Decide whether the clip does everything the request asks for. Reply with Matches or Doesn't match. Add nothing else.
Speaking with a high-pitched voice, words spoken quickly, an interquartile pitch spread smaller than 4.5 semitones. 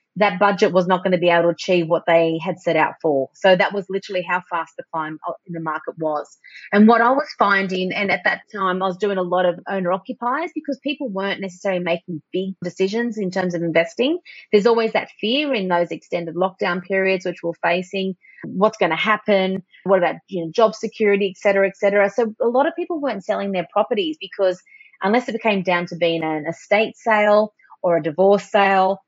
Matches